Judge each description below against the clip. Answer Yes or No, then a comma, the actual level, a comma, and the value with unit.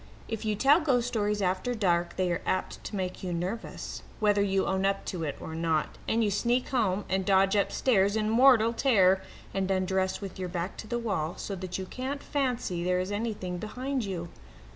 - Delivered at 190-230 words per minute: Yes, fast, 205 wpm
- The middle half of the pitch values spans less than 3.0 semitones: No, average, 3.7 semitones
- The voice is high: Yes, high, 195 Hz